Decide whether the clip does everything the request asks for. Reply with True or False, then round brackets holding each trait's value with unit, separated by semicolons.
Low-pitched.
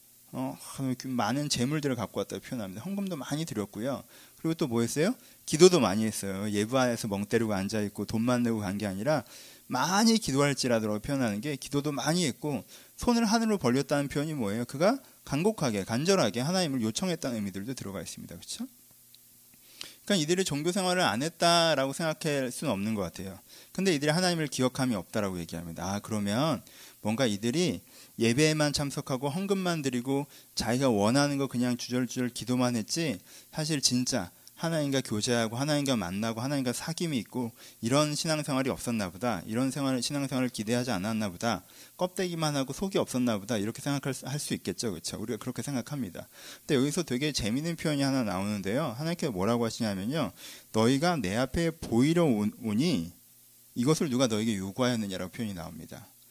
True (130 Hz)